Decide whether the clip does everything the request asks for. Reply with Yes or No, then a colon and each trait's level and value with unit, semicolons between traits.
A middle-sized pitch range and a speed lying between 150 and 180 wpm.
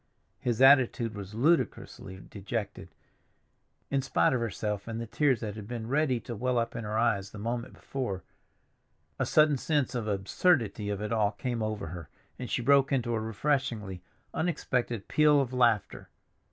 Yes: average, 4.0 semitones; average, 170 wpm